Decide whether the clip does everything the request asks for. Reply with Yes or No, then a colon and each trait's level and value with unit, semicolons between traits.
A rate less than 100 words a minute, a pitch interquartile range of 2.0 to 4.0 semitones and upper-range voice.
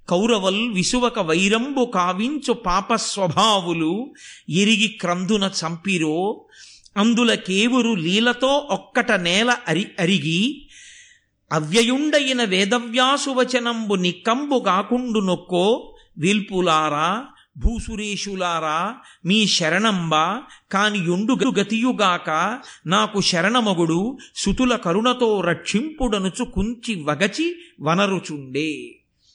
No: slow, 70 wpm; average, 5.3 semitones; high, 210 Hz